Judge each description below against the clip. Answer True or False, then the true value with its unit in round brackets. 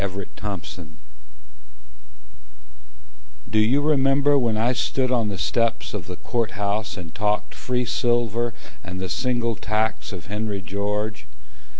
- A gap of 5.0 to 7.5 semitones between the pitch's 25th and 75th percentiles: False (3.3 semitones)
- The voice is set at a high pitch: False (110 Hz)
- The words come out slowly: True (130 wpm)